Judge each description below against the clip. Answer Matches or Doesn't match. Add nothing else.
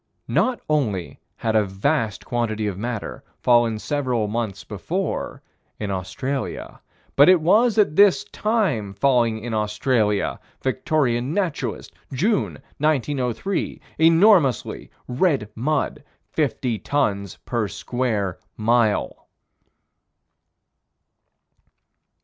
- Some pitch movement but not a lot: Doesn't match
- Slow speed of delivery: Matches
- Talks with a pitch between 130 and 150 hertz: Doesn't match